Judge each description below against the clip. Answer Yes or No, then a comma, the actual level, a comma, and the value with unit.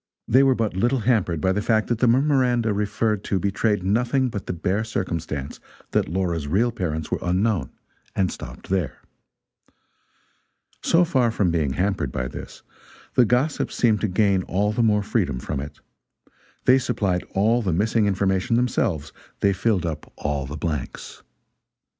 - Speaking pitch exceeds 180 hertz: No, low, 100 Hz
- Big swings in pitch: No, average, 4.7 semitones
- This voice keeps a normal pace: Yes, average, 160 wpm